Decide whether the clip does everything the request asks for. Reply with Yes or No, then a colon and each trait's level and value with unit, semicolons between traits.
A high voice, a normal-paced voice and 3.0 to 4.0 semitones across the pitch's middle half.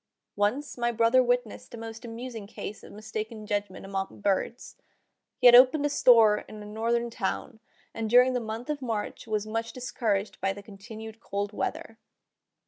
No: high, 225 Hz; average, 170 wpm; narrow, 2.5 semitones